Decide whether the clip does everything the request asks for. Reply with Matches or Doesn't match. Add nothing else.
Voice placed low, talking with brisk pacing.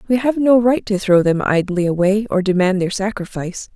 Doesn't match